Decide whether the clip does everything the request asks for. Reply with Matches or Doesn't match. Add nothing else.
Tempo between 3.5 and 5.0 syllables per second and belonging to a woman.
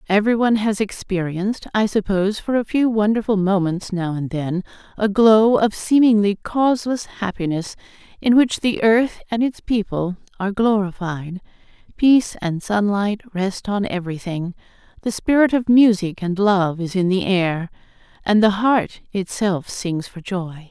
Matches